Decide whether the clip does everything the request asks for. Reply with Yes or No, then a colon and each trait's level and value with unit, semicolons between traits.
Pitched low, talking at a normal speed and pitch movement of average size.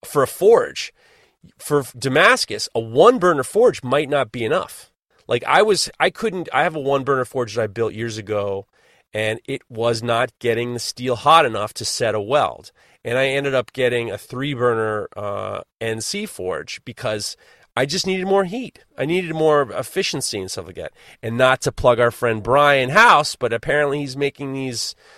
Yes: low, 130 Hz; average, 190 wpm; average, 4.0 semitones